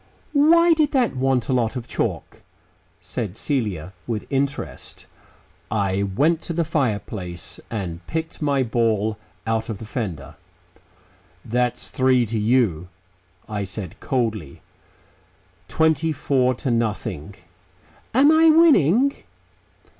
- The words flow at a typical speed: No, slow, 115 wpm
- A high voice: No, low, 125 Hz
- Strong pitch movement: Yes, wide, 6.7 semitones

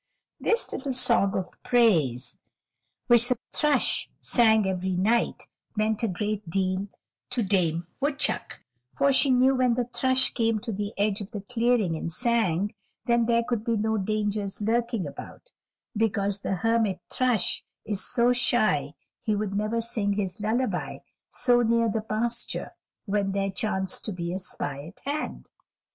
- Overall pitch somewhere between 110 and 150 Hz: No, high, 215 Hz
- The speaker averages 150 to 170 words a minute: Yes, average, 155 wpm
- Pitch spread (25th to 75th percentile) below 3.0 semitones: No, average, 3.4 semitones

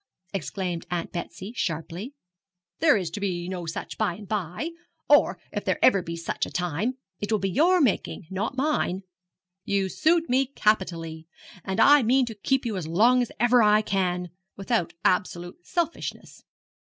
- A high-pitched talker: Yes, high, 200 Hz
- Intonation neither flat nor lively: No, wide, 6.0 semitones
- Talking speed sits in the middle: Yes, average, 170 wpm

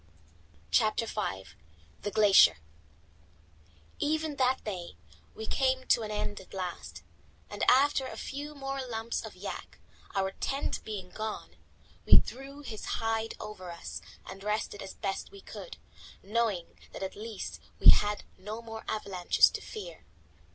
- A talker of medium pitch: No, high, 215 Hz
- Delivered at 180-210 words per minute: No, average, 140 wpm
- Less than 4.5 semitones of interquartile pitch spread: No, average, 5.0 semitones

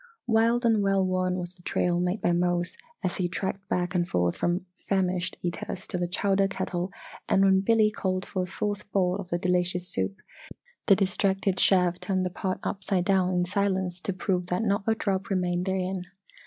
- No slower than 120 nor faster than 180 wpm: No, average, 195 wpm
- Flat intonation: Yes, narrow, 1.7 semitones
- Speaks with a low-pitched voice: No, medium, 185 Hz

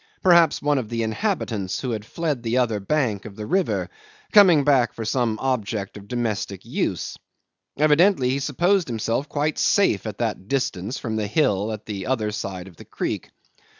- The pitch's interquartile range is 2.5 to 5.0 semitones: No, wide, 5.6 semitones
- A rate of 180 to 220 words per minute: Yes, average, 185 wpm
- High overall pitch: No, low, 120 Hz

